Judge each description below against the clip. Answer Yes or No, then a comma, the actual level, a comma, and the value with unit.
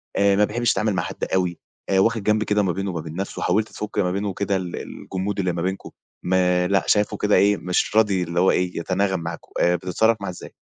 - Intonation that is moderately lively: No, narrow, 2.3 semitones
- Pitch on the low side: Yes, very low, 95 Hz